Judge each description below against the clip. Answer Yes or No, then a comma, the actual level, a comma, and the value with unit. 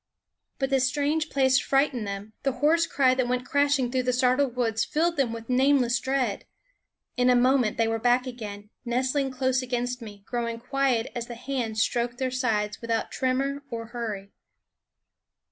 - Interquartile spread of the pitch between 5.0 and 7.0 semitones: No, narrow, 2.5 semitones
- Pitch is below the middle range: No, very high, 250 Hz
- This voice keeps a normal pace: Yes, average, 170 wpm